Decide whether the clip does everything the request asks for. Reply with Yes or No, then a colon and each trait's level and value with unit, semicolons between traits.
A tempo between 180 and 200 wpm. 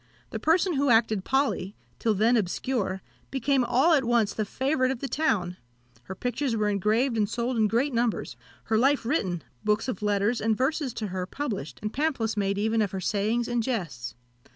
Yes: average, 190 wpm